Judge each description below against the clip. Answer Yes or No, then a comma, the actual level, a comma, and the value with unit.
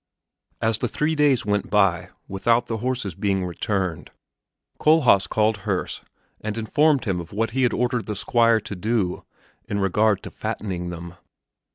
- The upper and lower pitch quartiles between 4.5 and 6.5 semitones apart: No, average, 3.5 semitones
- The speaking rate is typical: Yes, average, 160 wpm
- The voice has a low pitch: Yes, low, 105 Hz